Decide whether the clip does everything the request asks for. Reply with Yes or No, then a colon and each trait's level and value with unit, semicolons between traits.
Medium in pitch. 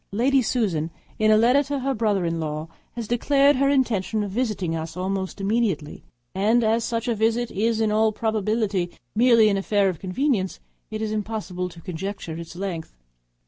No: high, 215 Hz